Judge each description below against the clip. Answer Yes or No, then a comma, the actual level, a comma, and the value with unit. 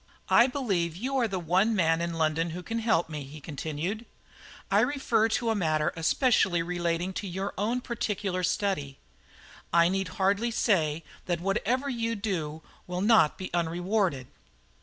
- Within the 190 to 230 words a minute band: No, average, 160 wpm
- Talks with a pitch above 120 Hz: Yes, medium, 185 Hz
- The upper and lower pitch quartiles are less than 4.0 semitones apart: No, average, 5.0 semitones